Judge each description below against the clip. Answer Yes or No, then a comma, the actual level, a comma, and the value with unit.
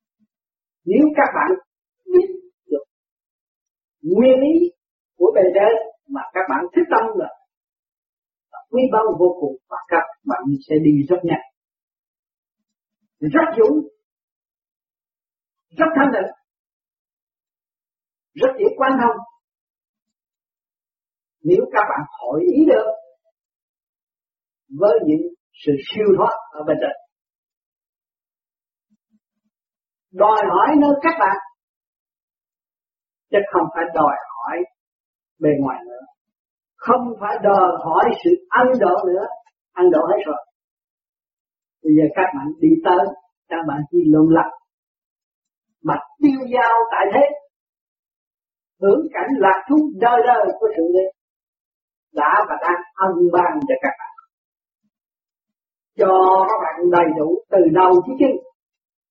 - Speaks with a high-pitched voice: Yes, high, 230 Hz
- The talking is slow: Yes, slow, 120 wpm